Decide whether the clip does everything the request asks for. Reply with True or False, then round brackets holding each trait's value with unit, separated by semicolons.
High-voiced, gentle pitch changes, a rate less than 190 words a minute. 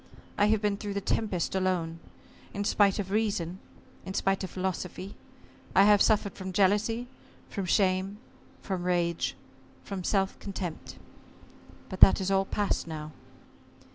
True (195 Hz; 1.9 semitones; 140 wpm)